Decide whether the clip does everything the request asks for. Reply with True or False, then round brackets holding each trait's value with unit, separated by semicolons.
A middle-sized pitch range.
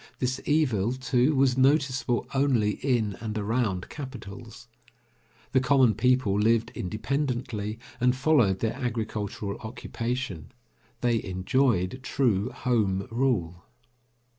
True (3.7 semitones)